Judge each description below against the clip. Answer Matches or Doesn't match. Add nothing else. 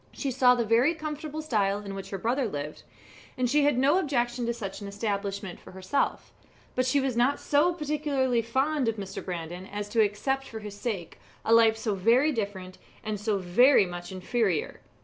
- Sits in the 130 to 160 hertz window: Doesn't match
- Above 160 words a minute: Matches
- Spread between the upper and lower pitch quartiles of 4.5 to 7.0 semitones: Matches